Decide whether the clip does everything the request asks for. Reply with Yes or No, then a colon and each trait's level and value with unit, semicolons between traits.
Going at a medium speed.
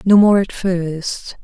Yes: average, 170 wpm